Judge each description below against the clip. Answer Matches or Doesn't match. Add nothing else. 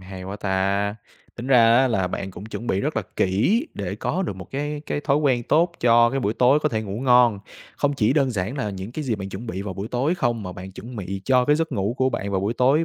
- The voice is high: Doesn't match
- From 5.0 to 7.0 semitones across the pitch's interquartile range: Matches